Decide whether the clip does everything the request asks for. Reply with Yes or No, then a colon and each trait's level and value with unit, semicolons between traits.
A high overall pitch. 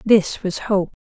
Yes: high, 200 Hz